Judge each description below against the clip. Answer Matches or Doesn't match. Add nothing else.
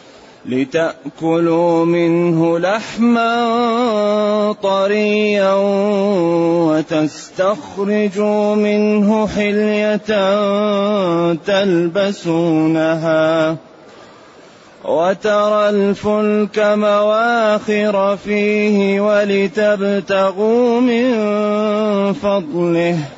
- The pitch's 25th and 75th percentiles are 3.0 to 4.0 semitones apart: Matches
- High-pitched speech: Matches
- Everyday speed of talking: Doesn't match